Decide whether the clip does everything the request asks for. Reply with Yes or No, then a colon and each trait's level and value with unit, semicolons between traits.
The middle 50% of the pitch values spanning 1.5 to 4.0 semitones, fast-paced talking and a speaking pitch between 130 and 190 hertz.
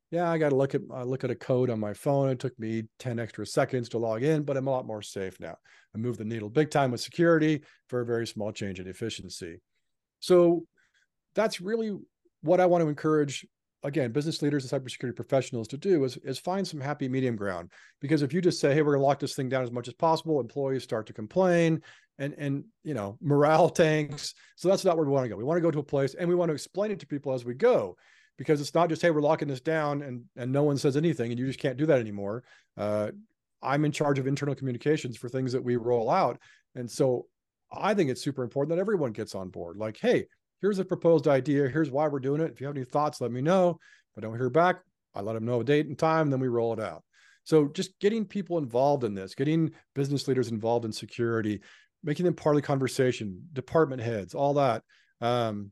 No: average, 4.7 semitones; fast, 245 wpm; medium, 140 Hz